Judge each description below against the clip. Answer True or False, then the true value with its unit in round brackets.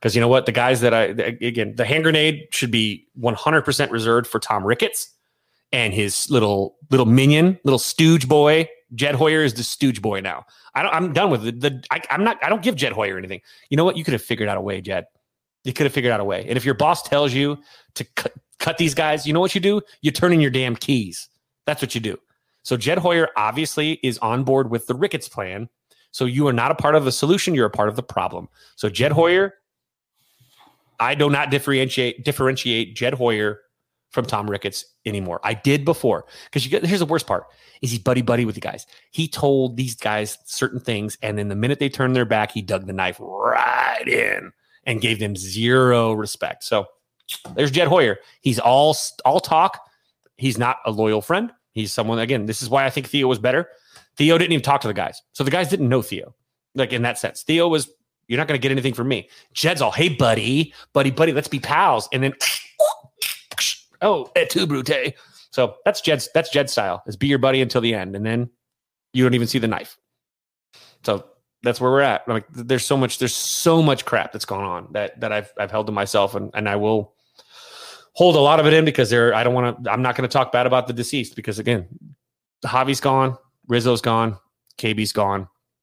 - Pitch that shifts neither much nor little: True (4.3 semitones)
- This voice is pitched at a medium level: False (130 Hz)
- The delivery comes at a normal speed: False (225 wpm)